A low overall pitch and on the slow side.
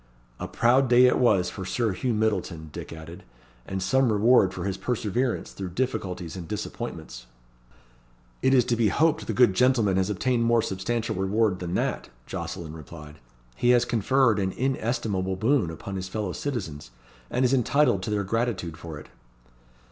No: low, 105 Hz; average, 170 wpm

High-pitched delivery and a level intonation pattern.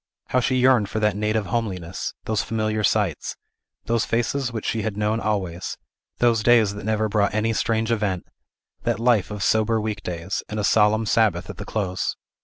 No: low, 110 Hz; narrow, 1.9 semitones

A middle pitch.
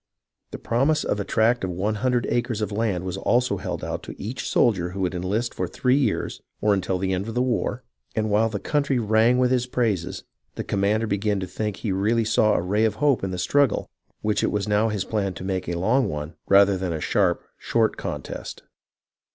No: low, 105 Hz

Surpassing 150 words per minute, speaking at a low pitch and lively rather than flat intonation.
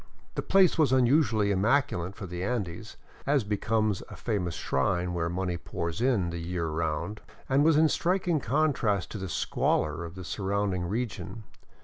Yes: average, 165 wpm; low, 100 Hz; wide, 6.5 semitones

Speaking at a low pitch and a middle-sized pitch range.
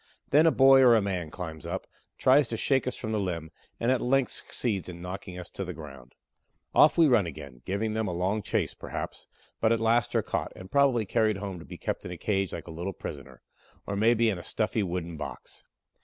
Yes: low, 100 Hz; average, 4.9 semitones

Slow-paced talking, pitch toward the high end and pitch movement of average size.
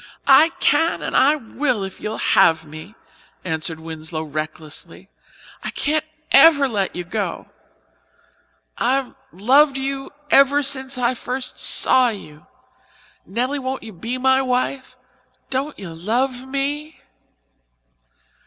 No: slow, 120 wpm; very high, 255 Hz; wide, 6.4 semitones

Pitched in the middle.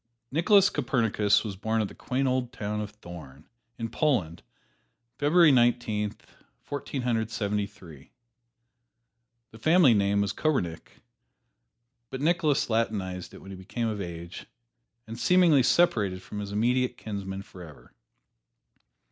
No: low, 110 Hz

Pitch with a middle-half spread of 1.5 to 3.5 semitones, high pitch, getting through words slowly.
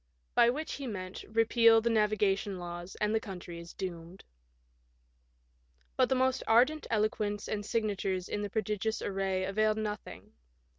No: average, 2.8 semitones; high, 210 Hz; average, 150 wpm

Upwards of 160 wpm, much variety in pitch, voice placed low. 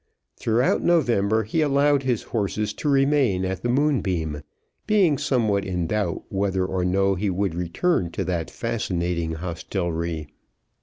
No: average, 140 wpm; wide, 6.6 semitones; low, 100 Hz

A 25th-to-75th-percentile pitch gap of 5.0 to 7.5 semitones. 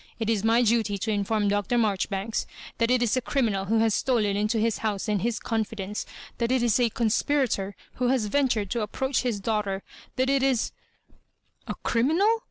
No: average, 3.0 semitones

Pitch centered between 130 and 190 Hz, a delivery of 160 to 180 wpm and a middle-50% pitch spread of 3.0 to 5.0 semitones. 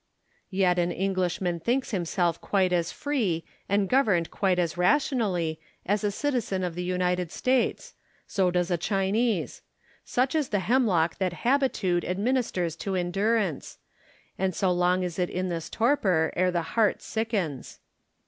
No: medium, 185 Hz; average, 150 wpm; average, 3.9 semitones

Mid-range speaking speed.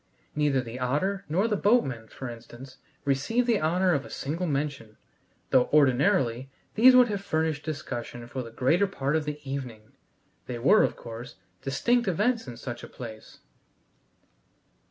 Yes: average, 155 wpm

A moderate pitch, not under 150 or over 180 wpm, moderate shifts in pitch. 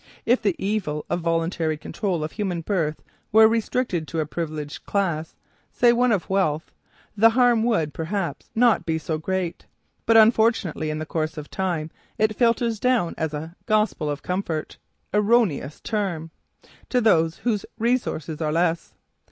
No: medium, 180 Hz; average, 160 wpm; wide, 5.7 semitones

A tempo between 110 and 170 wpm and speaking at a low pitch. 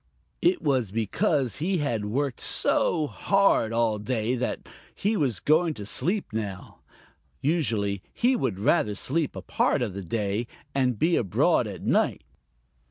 Yes: average, 150 wpm; low, 125 Hz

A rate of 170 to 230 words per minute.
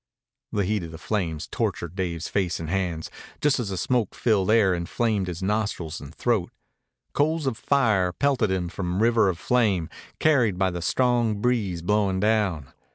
Yes: average, 175 wpm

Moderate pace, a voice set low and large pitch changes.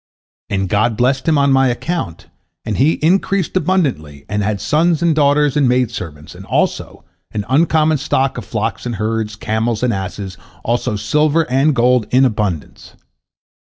Yes: average, 160 wpm; low, 125 Hz; wide, 6.0 semitones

